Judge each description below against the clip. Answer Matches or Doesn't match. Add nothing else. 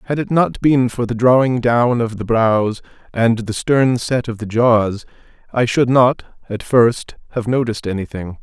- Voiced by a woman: Doesn't match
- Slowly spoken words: Doesn't match